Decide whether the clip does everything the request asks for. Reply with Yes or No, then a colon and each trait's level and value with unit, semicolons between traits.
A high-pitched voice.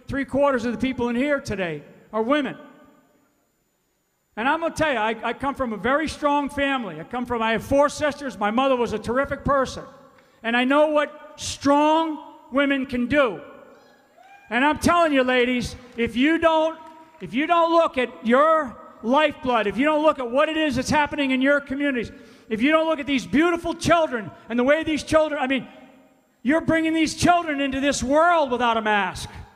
Yes: very high, 280 Hz